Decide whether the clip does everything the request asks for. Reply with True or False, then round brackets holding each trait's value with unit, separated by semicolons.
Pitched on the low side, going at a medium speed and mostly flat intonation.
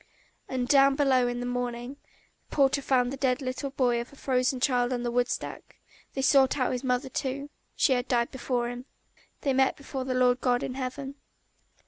False (255 Hz; 195 wpm; 1.6 semitones)